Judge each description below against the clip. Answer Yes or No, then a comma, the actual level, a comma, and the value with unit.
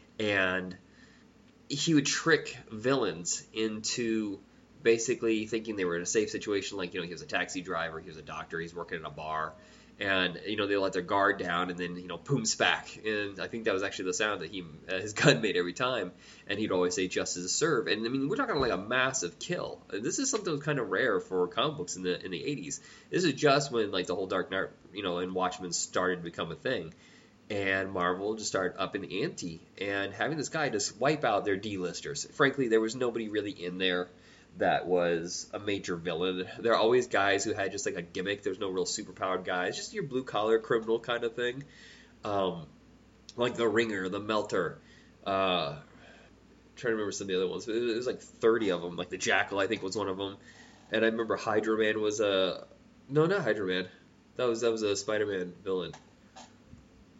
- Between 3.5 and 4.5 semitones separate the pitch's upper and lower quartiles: Yes, average, 4.2 semitones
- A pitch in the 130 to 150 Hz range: No, low, 105 Hz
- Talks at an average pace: No, fast, 220 wpm